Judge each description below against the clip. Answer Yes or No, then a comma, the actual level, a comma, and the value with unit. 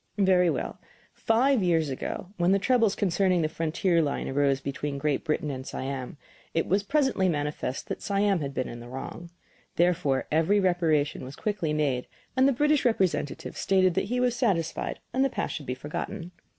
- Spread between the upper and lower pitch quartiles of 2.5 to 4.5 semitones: No, wide, 5.4 semitones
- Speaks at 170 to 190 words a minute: Yes, average, 180 wpm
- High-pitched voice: No, medium, 170 Hz